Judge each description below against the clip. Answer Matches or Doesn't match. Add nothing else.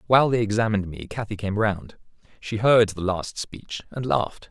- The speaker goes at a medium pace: Matches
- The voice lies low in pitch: Matches